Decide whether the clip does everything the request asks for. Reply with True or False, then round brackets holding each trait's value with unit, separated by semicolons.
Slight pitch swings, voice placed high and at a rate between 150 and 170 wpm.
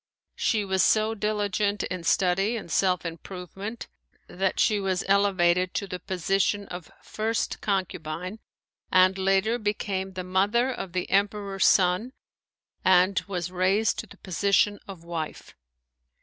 False (2.1 semitones; 195 Hz; 135 wpm)